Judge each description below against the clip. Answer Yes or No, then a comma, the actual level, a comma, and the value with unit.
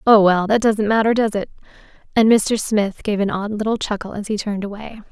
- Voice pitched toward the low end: No, high, 210 Hz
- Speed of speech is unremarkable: No, fast, 225 wpm